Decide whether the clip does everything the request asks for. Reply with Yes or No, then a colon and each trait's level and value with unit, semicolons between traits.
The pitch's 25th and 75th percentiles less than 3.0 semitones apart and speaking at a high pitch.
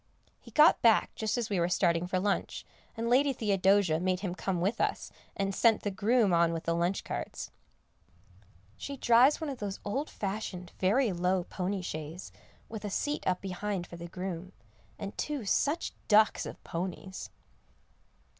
No: average, 3.8 semitones; high, 195 Hz